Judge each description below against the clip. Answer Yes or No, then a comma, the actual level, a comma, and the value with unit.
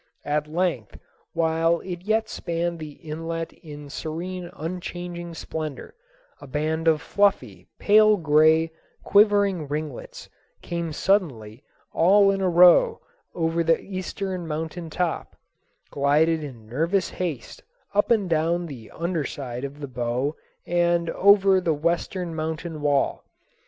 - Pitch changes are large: No, average, 3.1 semitones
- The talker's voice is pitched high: No, medium, 165 Hz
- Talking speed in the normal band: No, slow, 125 wpm